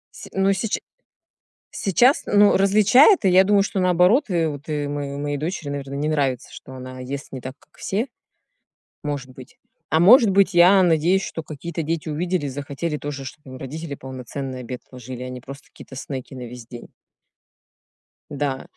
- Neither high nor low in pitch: Yes, medium, 145 Hz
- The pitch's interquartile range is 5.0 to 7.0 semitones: Yes, wide, 5.6 semitones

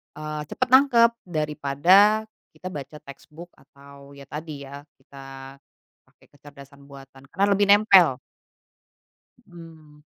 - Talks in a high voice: No, medium, 150 Hz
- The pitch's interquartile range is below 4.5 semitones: No, average, 4.8 semitones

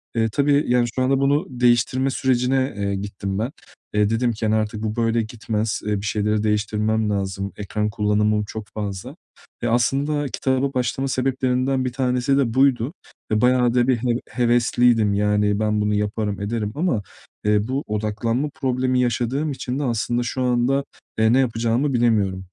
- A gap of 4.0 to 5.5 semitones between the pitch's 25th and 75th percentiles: No, average, 3.3 semitones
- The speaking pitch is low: Yes, low, 115 Hz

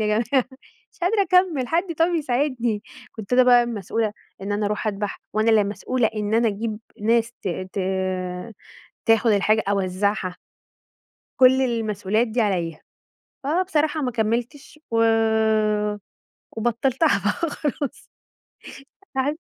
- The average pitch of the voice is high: Yes, high, 230 Hz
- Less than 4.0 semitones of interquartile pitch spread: No, average, 4.3 semitones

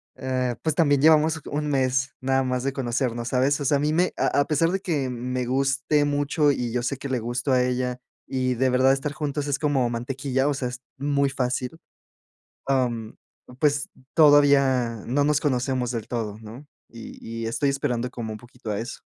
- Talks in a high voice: No, low, 130 Hz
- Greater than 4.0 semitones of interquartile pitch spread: No, narrow, 2.6 semitones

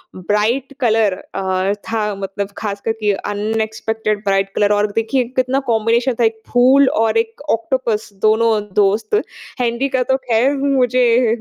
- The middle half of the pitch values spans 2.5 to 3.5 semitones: Yes, average, 2.9 semitones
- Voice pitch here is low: No, high, 225 Hz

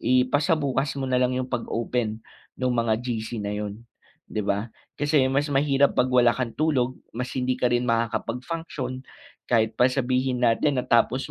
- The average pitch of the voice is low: Yes, low, 125 Hz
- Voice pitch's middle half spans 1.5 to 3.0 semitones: Yes, narrow, 2.4 semitones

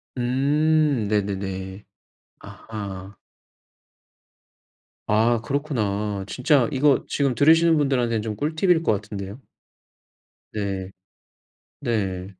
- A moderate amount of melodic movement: No, wide, 6.1 semitones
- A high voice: No, low, 115 Hz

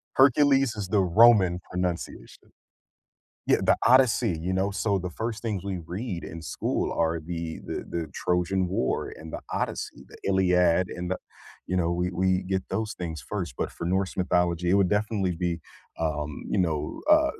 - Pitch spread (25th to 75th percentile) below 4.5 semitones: Yes, average, 2.9 semitones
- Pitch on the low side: Yes, very low, 90 Hz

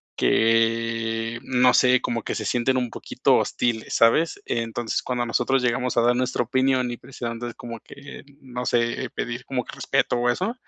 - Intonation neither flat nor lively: No, narrow, 1.6 semitones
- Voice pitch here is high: No, low, 120 Hz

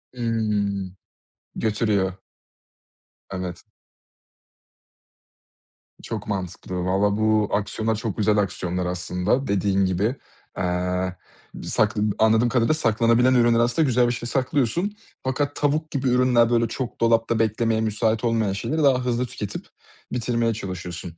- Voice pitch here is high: No, low, 110 Hz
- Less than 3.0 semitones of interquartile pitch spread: No, average, 3.6 semitones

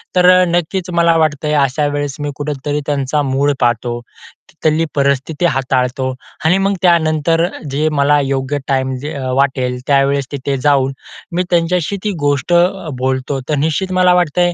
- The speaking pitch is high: No, medium, 145 Hz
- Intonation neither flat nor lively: Yes, average, 3.7 semitones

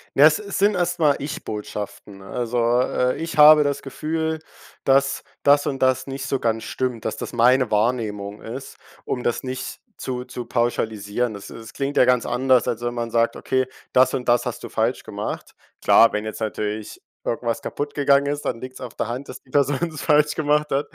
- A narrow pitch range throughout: No, average, 3.6 semitones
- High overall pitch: No, low, 130 Hz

